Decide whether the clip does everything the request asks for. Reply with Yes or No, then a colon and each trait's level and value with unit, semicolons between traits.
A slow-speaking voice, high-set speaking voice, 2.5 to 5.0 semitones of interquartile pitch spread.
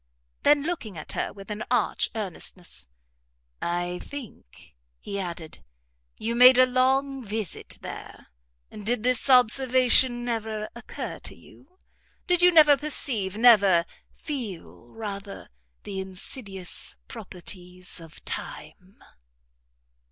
No: slow, 110 wpm; high, 215 Hz; wide, 5.5 semitones